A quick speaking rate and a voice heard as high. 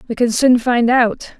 Yes: fast, 215 wpm; high, 240 Hz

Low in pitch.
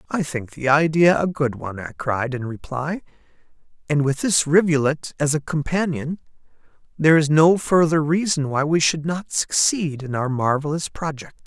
No: medium, 150 Hz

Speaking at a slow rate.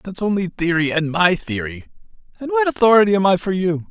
No: average, 200 wpm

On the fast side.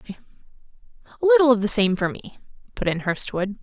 No: average, 165 wpm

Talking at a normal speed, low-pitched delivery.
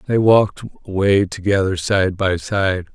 Yes: average, 145 wpm; low, 100 Hz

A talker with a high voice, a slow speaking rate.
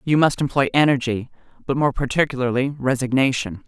No: low, 130 Hz; slow, 130 wpm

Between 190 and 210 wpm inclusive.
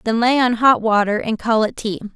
No: fast, 250 wpm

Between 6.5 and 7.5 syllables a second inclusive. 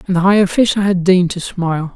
Yes: 6.6 syllables/s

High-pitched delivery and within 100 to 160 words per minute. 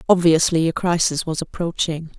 No: medium, 165 Hz; average, 140 wpm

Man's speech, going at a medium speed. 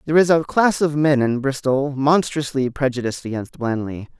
Yes: male; average, 170 wpm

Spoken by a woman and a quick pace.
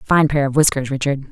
Yes: female; fast, 275 wpm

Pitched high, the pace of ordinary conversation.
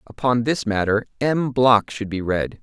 No: low, 115 Hz; average, 185 wpm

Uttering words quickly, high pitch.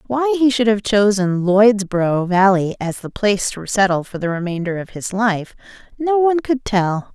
No: average, 185 wpm; high, 210 Hz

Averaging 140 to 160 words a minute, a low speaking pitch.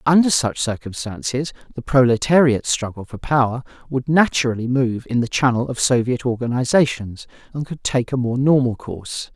Yes: average, 155 wpm; low, 125 Hz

